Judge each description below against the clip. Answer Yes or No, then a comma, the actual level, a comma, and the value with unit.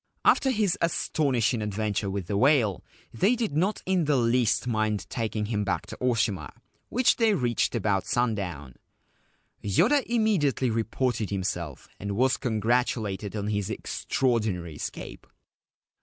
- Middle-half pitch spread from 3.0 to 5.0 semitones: No, wide, 5.4 semitones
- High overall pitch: No, low, 115 Hz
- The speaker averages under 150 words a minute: Yes, slow, 135 wpm